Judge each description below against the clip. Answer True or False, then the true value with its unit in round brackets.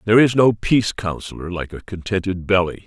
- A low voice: True (100 Hz)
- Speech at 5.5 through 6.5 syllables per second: True (5.9 syllables/s)